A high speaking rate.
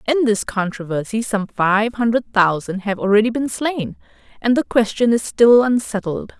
No: average, 160 wpm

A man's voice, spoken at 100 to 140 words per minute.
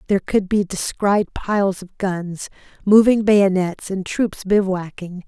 No: female; slow, 135 wpm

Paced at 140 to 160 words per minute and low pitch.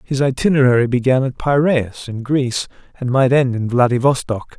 Yes: average, 155 wpm; low, 130 Hz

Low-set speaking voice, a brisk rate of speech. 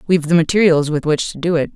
No: medium, 165 Hz; fast, 275 wpm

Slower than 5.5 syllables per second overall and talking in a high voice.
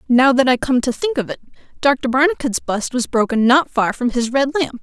Yes: 5.2 syllables/s; very high, 260 Hz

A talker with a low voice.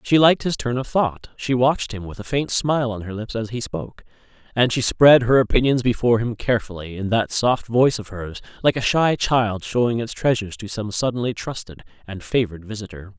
Yes: low, 115 Hz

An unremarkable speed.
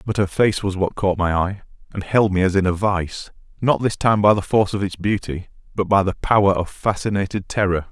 No: fast, 235 wpm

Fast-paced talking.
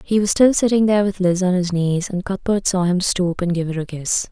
Yes: fast, 280 wpm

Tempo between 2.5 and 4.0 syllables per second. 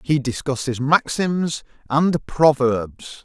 Yes: 3.2 syllables/s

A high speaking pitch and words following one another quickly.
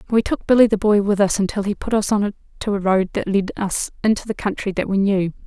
Yes: high, 200 Hz; fast, 265 wpm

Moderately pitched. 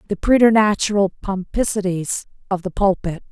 No: high, 195 Hz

